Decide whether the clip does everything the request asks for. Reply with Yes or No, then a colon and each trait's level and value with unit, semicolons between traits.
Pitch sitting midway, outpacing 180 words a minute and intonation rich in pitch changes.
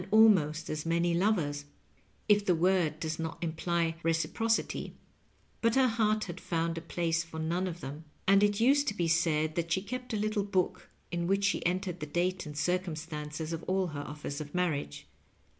No: medium, 170 Hz; average, 190 wpm; average, 3.7 semitones